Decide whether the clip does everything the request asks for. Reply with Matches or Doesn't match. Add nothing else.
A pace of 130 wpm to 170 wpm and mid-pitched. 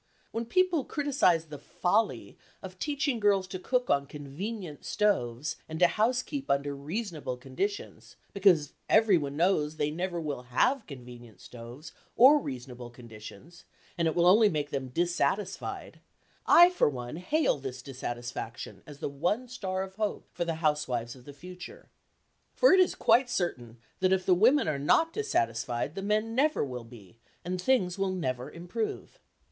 Matches